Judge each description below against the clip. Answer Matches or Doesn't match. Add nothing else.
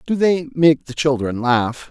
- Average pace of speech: Matches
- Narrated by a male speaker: Matches